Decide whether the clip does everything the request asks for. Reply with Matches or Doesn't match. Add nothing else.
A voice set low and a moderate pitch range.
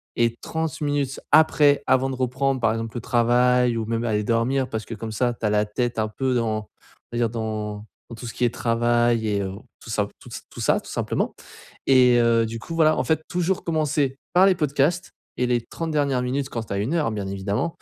Matches